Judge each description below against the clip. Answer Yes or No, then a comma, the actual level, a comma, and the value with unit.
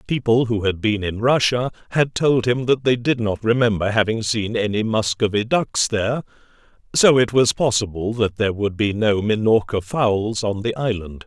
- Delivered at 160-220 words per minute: Yes, average, 180 wpm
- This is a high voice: No, low, 110 Hz